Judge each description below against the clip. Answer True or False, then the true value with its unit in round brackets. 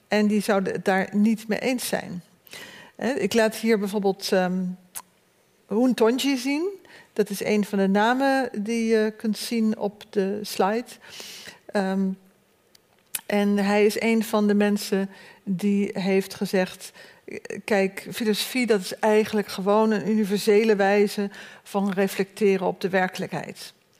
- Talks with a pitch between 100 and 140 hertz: False (205 Hz)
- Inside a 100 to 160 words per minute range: True (140 wpm)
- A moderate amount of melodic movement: False (1.8 semitones)